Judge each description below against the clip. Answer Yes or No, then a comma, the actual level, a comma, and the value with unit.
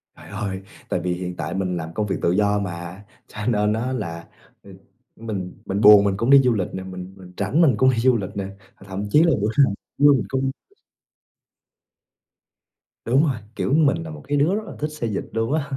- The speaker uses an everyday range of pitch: No, wide, 6.0 semitones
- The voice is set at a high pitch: No, low, 105 Hz